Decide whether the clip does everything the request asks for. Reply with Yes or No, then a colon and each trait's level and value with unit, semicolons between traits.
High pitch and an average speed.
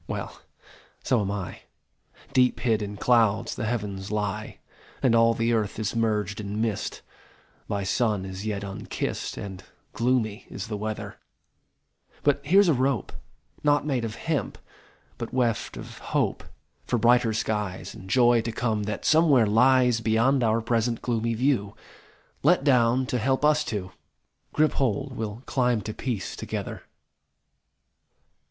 No: low, 115 Hz; average, 150 wpm